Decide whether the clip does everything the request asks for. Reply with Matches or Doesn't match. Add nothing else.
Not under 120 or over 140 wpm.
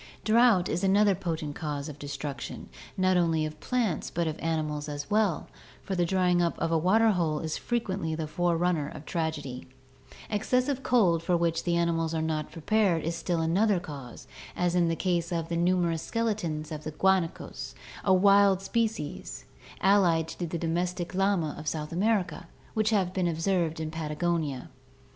Doesn't match